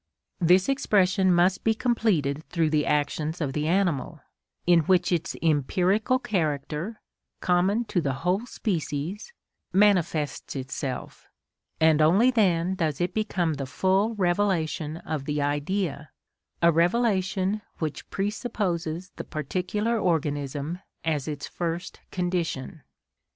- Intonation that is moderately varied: Yes, average, 4.3 semitones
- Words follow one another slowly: Yes, slow, 120 wpm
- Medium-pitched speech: Yes, medium, 175 Hz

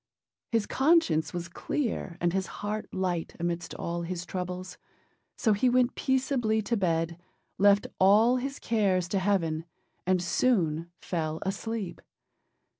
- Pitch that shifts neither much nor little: Yes, average, 4.7 semitones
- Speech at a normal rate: No, slow, 130 wpm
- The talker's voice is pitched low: No, high, 190 Hz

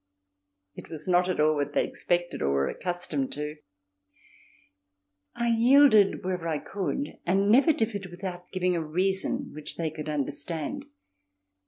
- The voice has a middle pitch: Yes, medium, 175 Hz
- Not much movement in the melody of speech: No, average, 4.4 semitones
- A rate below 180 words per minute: Yes, average, 145 wpm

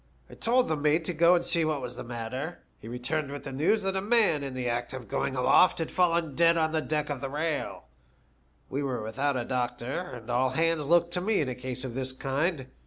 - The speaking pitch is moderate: Yes, medium, 145 Hz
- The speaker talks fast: Yes, fast, 240 wpm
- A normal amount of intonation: Yes, average, 4.7 semitones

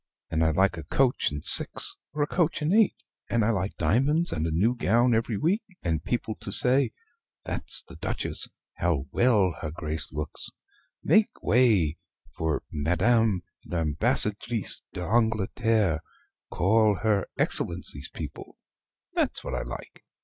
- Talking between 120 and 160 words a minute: Yes, average, 140 wpm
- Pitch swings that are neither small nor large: No, wide, 6.6 semitones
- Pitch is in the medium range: No, low, 105 Hz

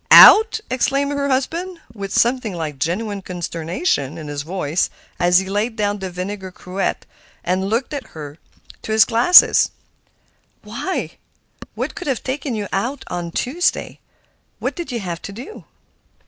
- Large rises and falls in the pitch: Yes, wide, 6.7 semitones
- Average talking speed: Yes, average, 150 wpm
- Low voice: No, high, 205 Hz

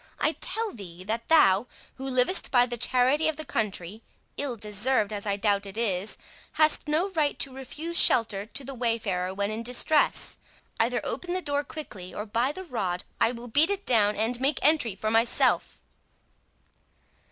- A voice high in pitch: Yes, high, 240 Hz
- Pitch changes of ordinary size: No, wide, 5.7 semitones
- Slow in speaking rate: No, average, 170 wpm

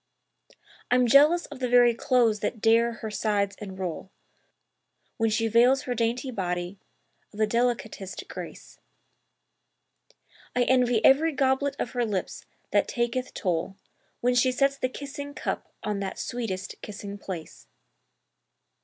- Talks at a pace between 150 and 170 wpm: No, slow, 135 wpm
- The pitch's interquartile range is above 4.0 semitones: No, average, 3.7 semitones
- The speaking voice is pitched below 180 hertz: No, high, 235 Hz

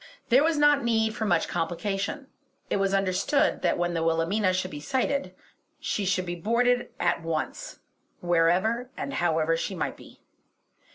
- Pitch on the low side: No, high, 195 Hz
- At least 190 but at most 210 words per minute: No, average, 160 wpm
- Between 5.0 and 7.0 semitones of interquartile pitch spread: Yes, wide, 5.6 semitones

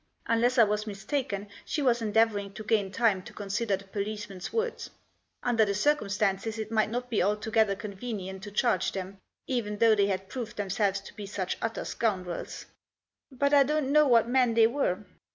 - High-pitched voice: Yes, high, 215 Hz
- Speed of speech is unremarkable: Yes, average, 190 wpm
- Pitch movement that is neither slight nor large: Yes, average, 3.0 semitones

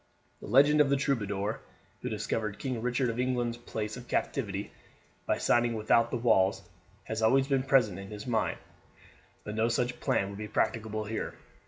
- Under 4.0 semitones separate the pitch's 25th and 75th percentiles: Yes, average, 2.9 semitones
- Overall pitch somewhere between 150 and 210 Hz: No, low, 115 Hz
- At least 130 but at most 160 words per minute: No, average, 175 wpm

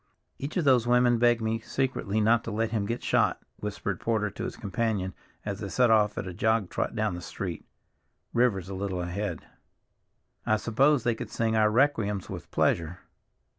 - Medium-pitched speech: No, low, 110 Hz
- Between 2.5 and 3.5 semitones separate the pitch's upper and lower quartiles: Yes, average, 2.8 semitones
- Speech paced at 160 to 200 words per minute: Yes, average, 185 wpm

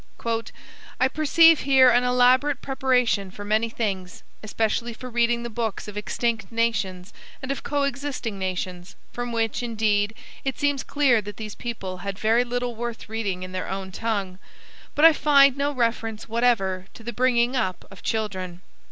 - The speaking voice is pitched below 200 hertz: No, high, 230 Hz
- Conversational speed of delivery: Yes, average, 160 wpm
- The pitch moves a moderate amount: Yes, average, 3.5 semitones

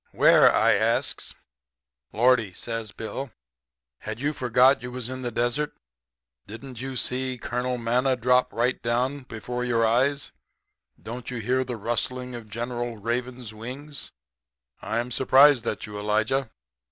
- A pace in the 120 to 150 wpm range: Yes, average, 140 wpm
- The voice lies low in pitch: Yes, low, 125 Hz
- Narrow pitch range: Yes, narrow, 1.9 semitones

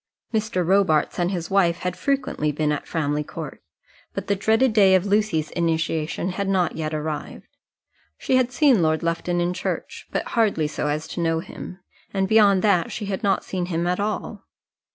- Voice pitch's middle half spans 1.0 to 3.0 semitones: No, average, 3.8 semitones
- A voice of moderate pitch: Yes, medium, 180 Hz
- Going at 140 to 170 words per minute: No, average, 185 wpm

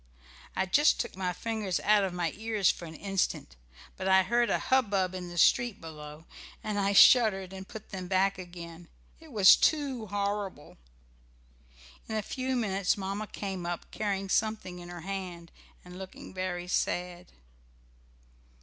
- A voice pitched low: No, high, 190 Hz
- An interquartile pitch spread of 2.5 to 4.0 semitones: Yes, average, 2.9 semitones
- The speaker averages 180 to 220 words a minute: No, average, 160 wpm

